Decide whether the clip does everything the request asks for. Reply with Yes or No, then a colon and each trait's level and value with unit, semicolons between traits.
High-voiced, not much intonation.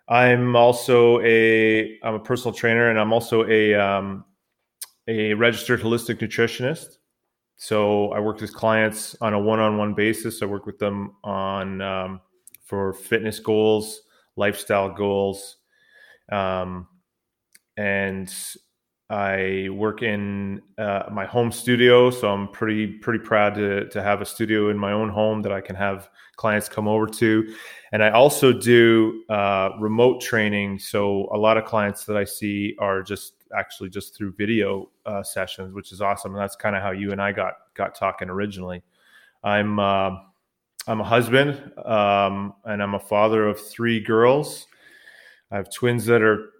No: low, 105 Hz; narrow, 2.2 semitones